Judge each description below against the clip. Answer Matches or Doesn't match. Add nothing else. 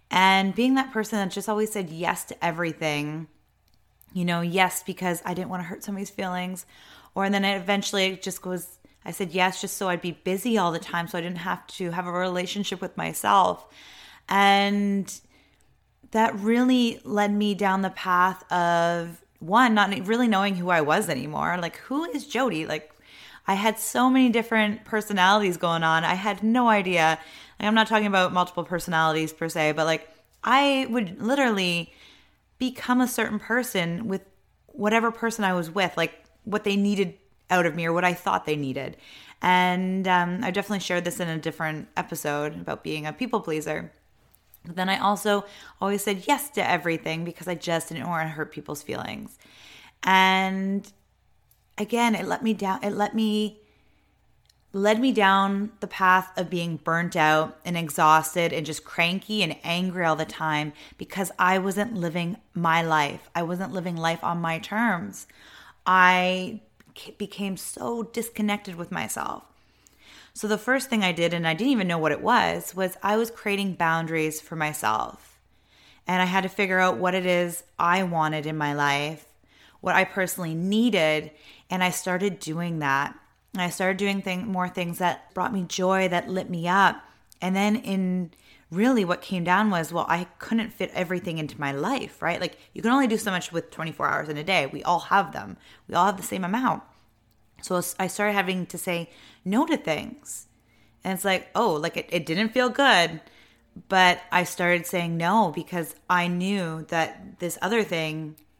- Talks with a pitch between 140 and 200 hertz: Matches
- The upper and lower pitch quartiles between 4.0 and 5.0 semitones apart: Doesn't match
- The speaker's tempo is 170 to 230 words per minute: Matches